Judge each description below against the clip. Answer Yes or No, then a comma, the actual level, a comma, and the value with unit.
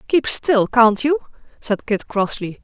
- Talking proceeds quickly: No, average, 160 wpm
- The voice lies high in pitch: Yes, high, 240 Hz